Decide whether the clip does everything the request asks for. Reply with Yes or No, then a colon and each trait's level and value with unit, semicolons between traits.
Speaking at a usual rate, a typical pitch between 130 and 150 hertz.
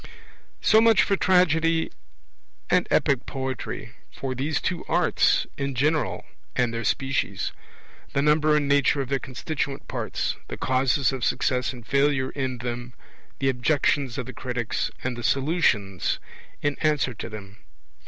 Yes: average, 145 wpm; low, 135 Hz